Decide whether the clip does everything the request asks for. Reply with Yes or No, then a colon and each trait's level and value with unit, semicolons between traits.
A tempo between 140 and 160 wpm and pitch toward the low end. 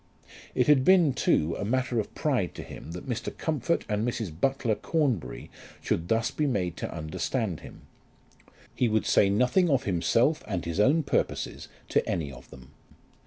No: average, 170 wpm; low, 115 Hz